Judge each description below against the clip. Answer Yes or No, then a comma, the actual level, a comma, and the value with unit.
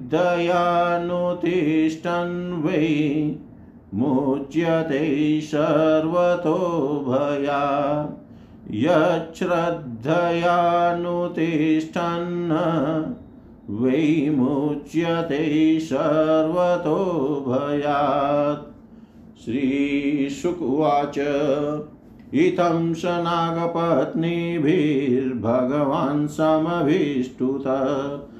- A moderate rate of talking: No, slow, 35 wpm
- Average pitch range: Yes, average, 3.1 semitones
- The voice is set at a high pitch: No, medium, 155 Hz